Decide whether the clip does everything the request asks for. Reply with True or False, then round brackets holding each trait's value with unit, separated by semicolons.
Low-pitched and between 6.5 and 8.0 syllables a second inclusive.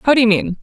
False (230 Hz; 7.0 syllables/s)